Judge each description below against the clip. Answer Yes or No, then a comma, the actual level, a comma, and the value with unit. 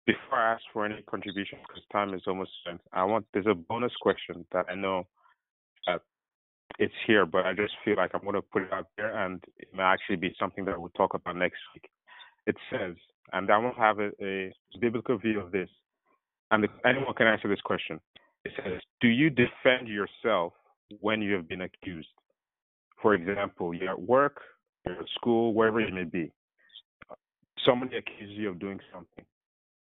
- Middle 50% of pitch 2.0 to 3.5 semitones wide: Yes, average, 2.8 semitones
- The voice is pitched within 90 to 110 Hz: Yes, low, 105 Hz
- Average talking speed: Yes, average, 190 wpm